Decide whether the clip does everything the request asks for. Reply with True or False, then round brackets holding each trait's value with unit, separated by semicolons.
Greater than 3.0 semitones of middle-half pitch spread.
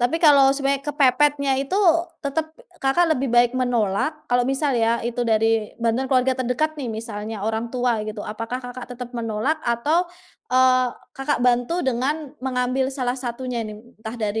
False (2.5 semitones)